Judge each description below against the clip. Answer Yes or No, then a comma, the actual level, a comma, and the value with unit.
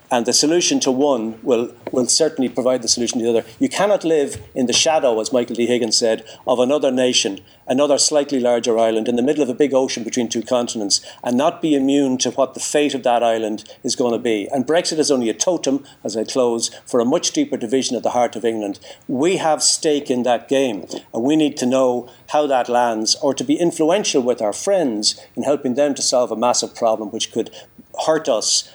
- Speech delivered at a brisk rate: Yes, fast, 225 wpm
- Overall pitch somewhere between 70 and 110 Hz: No, low, 125 Hz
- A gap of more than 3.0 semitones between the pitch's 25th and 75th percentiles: Yes, average, 3.7 semitones